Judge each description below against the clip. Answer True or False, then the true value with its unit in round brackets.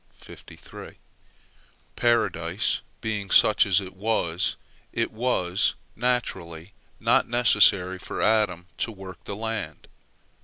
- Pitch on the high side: False (100 Hz)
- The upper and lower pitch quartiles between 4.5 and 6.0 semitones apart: False (3.9 semitones)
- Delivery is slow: True (100 wpm)